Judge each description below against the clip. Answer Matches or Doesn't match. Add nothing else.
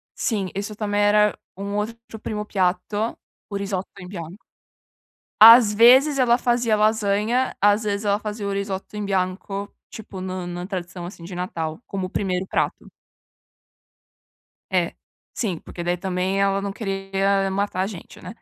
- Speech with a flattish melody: Matches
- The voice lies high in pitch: Matches